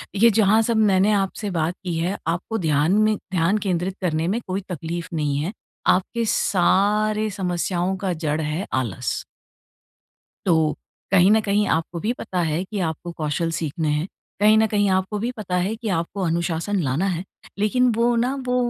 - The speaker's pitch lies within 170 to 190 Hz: Yes, medium, 185 Hz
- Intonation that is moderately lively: Yes, average, 4.1 semitones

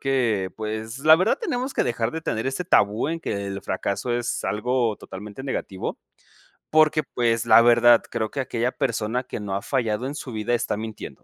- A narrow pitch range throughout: No, average, 3.7 semitones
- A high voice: No, low, 120 Hz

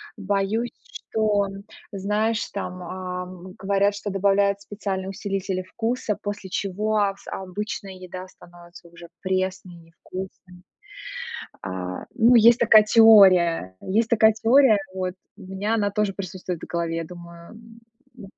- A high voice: Yes, high, 195 Hz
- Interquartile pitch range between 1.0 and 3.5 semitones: Yes, narrow, 2.5 semitones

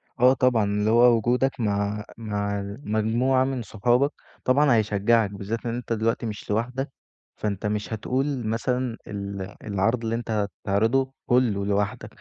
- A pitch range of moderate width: Yes, average, 3.2 semitones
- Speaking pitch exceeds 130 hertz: No, low, 115 Hz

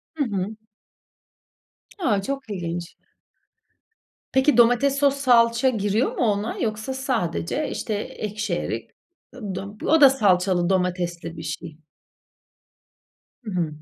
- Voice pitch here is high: Yes, high, 210 Hz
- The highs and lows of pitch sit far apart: Yes, wide, 6.1 semitones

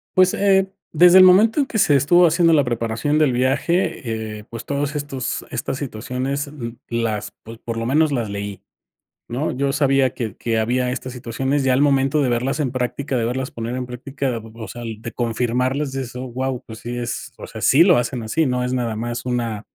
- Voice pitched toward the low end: Yes, low, 130 Hz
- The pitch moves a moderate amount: Yes, average, 3.4 semitones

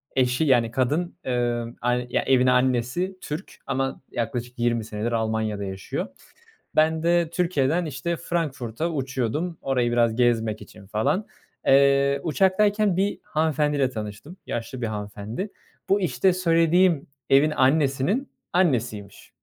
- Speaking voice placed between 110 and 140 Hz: Yes, low, 135 Hz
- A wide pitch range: Yes, wide, 5.8 semitones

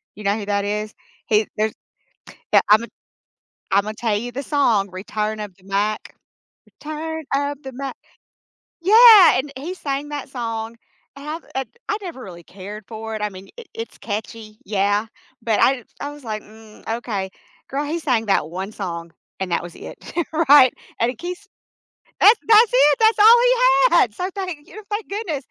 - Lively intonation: Yes, wide, 6.1 semitones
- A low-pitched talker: No, high, 235 Hz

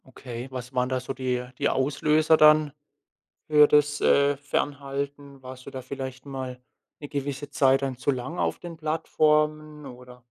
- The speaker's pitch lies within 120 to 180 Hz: Yes, medium, 140 Hz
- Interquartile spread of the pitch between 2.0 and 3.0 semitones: Yes, narrow, 2.5 semitones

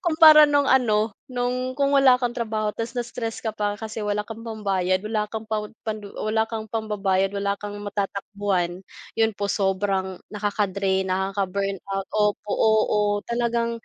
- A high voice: Yes, high, 210 Hz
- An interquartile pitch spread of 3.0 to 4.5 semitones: No, narrow, 2.4 semitones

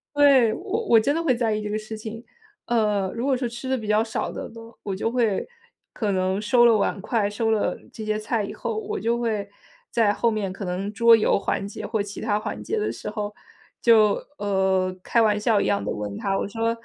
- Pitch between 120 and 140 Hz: No, high, 215 Hz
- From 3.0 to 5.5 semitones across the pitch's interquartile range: No, narrow, 2.4 semitones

